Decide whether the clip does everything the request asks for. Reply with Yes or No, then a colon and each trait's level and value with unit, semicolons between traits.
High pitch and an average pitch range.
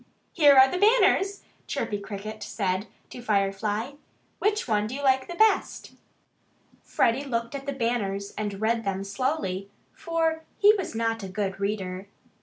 No: high, 225 Hz; wide, 6.0 semitones